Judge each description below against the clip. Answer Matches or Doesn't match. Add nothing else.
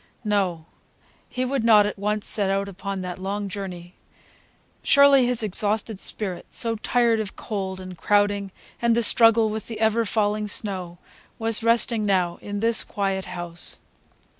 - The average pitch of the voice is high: Matches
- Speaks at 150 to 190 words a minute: Matches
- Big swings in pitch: Doesn't match